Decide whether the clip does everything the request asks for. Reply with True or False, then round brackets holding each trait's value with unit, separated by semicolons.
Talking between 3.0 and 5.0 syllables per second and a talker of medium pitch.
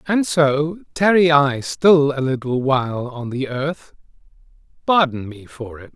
True (4.0 syllables/s; 145 Hz)